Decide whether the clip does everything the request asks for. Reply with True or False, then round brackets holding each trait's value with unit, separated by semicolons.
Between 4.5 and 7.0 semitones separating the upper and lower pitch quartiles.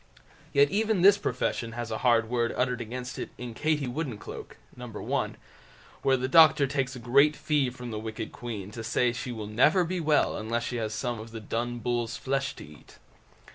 False (3.4 semitones)